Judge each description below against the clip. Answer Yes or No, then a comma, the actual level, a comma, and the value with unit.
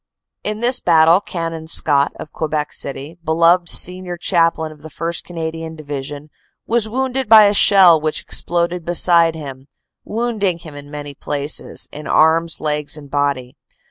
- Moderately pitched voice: Yes, medium, 165 Hz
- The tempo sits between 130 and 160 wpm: Yes, average, 150 wpm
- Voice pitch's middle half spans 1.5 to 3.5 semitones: Yes, average, 3.0 semitones